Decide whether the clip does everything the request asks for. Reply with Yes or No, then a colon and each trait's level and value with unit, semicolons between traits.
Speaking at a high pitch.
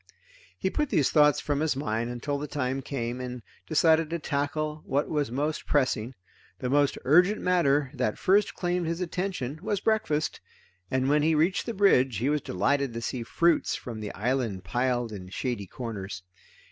No: medium, 140 Hz